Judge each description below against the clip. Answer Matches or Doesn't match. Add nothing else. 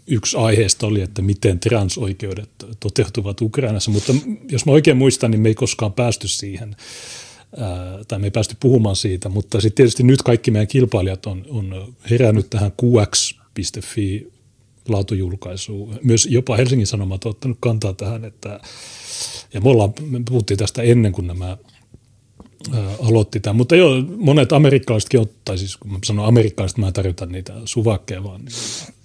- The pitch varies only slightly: Doesn't match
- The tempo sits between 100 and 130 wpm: Doesn't match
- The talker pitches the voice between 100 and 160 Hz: Matches